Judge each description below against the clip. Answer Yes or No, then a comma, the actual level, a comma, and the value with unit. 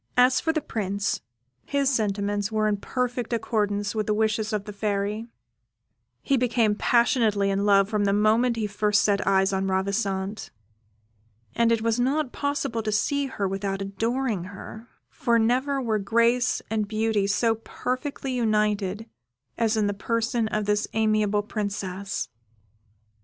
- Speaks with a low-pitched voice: No, high, 215 Hz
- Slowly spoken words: No, average, 150 wpm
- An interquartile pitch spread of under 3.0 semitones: Yes, narrow, 2.6 semitones